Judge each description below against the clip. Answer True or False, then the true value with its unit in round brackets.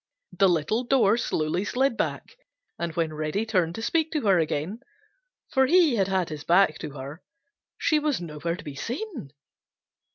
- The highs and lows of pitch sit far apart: True (7.7 semitones)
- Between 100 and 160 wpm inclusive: False (170 wpm)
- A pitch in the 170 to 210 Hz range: True (190 Hz)